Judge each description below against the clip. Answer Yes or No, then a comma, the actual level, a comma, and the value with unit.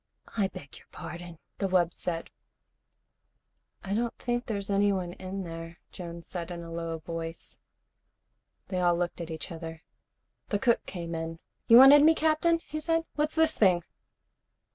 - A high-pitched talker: No, medium, 180 Hz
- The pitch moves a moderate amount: No, wide, 5.7 semitones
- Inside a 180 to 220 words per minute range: No, average, 160 wpm